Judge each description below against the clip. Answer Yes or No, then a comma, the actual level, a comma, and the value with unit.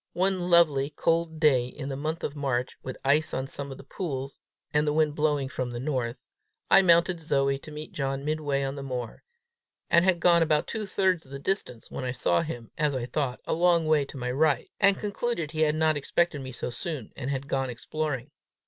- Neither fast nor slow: No, fast, 220 wpm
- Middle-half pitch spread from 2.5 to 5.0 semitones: Yes, average, 3.5 semitones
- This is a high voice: No, medium, 150 Hz